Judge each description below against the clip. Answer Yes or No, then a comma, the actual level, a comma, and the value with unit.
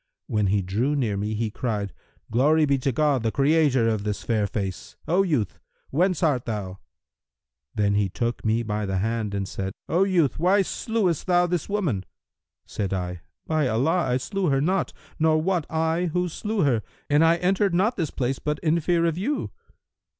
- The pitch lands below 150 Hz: Yes, medium, 140 Hz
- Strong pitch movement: Yes, wide, 8.1 semitones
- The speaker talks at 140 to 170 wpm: No, average, 185 wpm